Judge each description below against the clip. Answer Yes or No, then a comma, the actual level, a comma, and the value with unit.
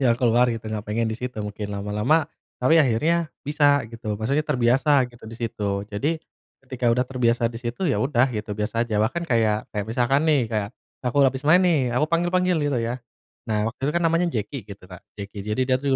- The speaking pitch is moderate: No, low, 120 Hz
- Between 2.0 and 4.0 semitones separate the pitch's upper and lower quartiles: No, average, 4.8 semitones